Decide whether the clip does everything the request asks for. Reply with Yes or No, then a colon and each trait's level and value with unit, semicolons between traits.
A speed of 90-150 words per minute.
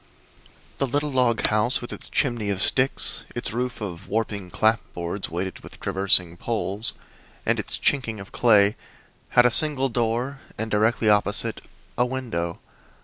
Yes: average, 145 wpm